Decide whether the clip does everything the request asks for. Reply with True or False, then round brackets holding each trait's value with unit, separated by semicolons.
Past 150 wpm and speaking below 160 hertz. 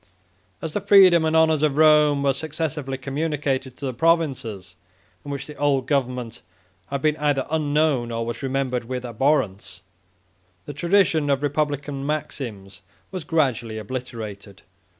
False (140 wpm; 140 Hz)